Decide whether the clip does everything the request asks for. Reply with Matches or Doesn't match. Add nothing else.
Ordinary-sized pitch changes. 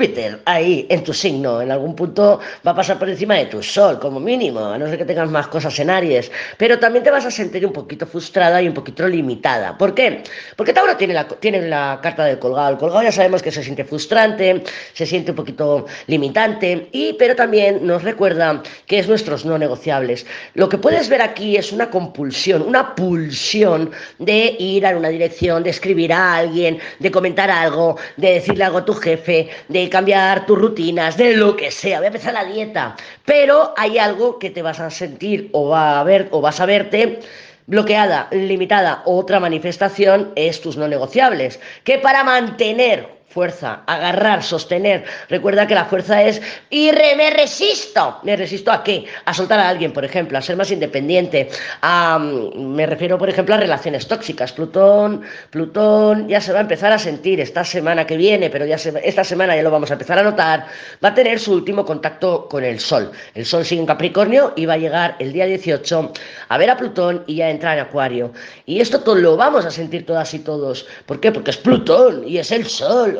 Matches